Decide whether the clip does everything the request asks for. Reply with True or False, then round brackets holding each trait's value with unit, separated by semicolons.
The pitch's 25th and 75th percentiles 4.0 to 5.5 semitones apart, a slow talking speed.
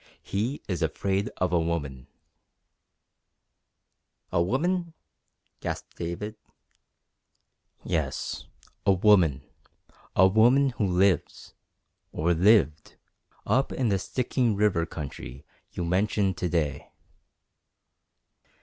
True (4.6 semitones; 95 wpm)